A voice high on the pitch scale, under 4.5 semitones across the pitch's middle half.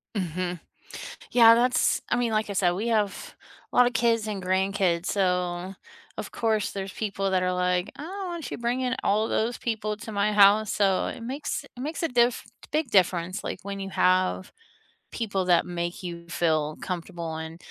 Yes: high, 200 Hz; average, 4.1 semitones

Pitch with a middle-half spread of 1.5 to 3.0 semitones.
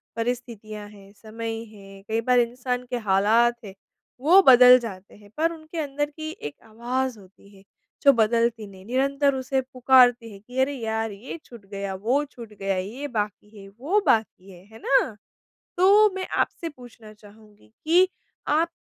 No: average, 4.1 semitones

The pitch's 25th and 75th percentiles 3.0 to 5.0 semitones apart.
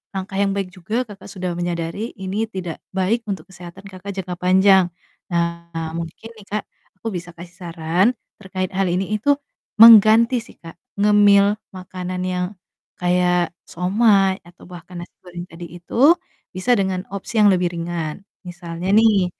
No: narrow, 2.4 semitones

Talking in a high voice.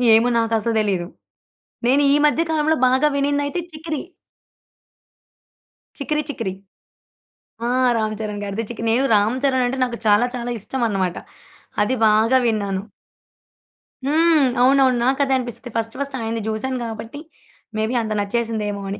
Yes: high, 235 Hz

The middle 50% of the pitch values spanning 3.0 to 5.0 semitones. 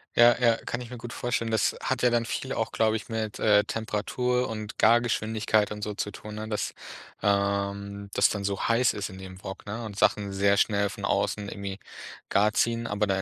No: narrow, 2.4 semitones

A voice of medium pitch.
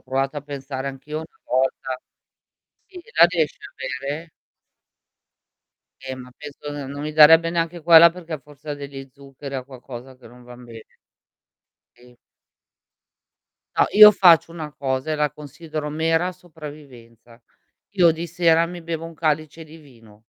Yes: medium, 150 Hz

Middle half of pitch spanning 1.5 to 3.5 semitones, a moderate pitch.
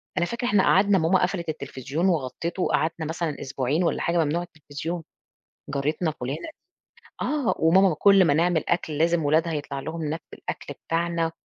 Yes: average, 2.7 semitones; medium, 165 Hz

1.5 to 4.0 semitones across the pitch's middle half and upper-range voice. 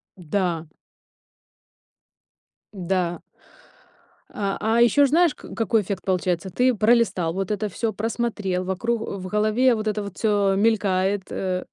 Yes: average, 3.3 semitones; high, 205 Hz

